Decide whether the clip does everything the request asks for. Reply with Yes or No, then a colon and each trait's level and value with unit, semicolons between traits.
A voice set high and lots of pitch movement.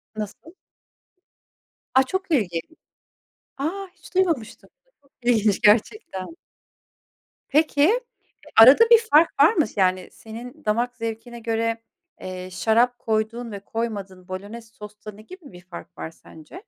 Yes: high, 230 Hz; wide, 5.7 semitones